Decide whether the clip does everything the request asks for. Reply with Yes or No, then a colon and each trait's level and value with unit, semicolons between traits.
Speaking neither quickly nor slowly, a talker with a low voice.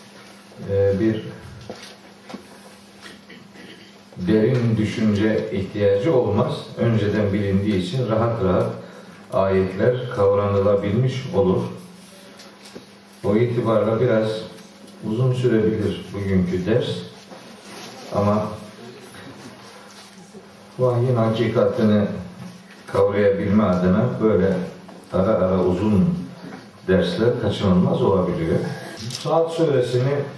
No: slow, 65 wpm; low, 110 Hz